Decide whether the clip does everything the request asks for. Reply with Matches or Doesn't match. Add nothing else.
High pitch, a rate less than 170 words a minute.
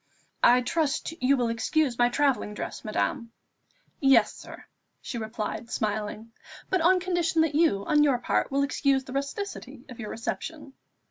Matches